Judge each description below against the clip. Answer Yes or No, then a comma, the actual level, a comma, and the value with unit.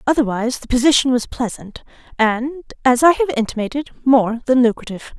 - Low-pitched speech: No, very high, 250 Hz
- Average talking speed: Yes, average, 150 wpm